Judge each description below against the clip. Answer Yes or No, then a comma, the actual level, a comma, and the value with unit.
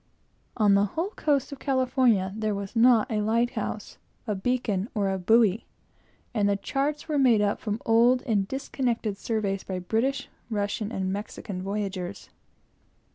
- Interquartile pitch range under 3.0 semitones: No, average, 3.8 semitones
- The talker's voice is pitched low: No, high, 215 Hz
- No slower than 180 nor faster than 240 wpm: No, average, 150 wpm